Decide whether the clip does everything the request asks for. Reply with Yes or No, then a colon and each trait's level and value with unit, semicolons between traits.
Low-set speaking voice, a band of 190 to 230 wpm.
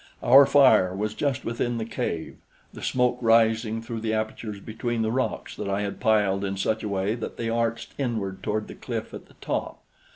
Yes: low, 110 Hz; average, 200 wpm